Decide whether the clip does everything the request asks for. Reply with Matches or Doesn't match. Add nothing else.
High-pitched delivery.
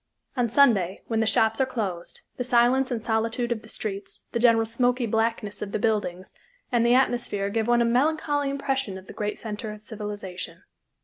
Matches